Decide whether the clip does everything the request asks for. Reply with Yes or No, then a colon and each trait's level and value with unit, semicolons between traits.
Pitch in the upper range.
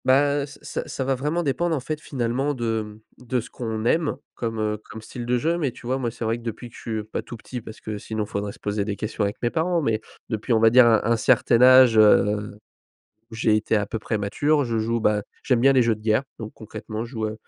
No: low, 115 Hz